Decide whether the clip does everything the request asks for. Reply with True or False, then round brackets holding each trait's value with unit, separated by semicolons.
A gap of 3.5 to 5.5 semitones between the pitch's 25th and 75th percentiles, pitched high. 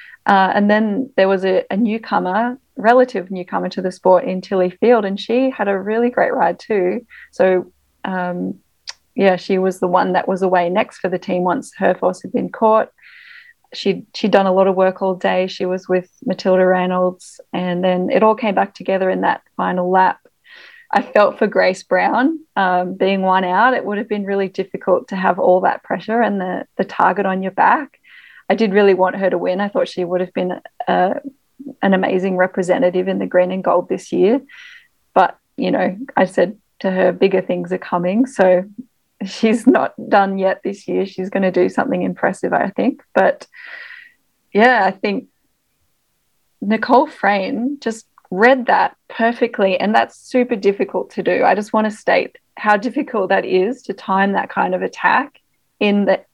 True (4.6 semitones; 195 Hz)